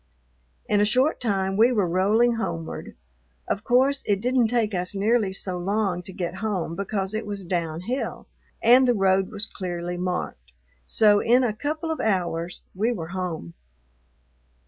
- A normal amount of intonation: Yes, average, 4.2 semitones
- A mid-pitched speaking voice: No, high, 200 Hz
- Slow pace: No, average, 160 wpm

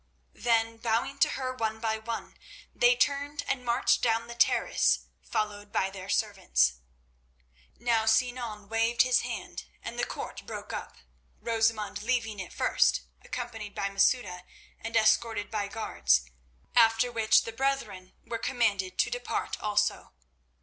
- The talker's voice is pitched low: No, high, 225 Hz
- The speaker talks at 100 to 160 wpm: Yes, average, 140 wpm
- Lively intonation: No, average, 2.7 semitones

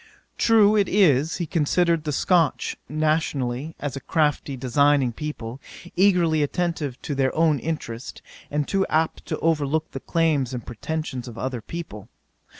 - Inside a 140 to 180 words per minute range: Yes, average, 150 wpm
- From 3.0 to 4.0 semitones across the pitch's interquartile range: Yes, average, 3.7 semitones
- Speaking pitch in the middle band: Yes, medium, 150 Hz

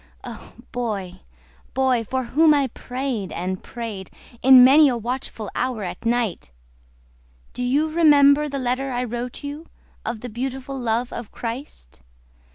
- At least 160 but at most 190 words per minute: No, average, 145 wpm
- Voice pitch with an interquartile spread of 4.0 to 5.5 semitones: No, average, 3.0 semitones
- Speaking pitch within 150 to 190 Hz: No, very high, 250 Hz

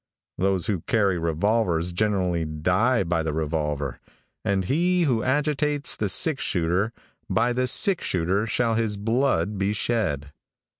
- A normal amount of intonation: No, wide, 6.2 semitones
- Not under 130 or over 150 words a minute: Yes, average, 140 wpm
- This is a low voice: Yes, low, 100 Hz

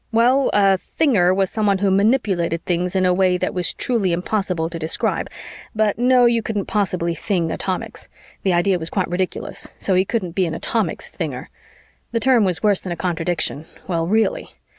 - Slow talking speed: No, average, 185 wpm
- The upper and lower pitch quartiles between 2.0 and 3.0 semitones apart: No, average, 3.5 semitones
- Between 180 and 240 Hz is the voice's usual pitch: Yes, high, 190 Hz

